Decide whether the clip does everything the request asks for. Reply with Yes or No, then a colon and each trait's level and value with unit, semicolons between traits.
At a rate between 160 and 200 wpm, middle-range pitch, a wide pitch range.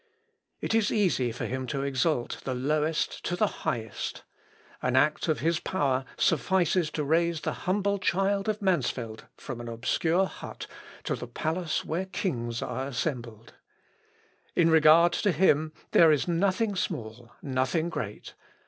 No: average, 150 wpm; medium, 155 Hz; wide, 5.9 semitones